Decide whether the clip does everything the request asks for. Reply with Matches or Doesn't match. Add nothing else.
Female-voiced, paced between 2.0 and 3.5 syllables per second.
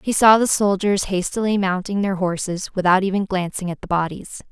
Doesn't match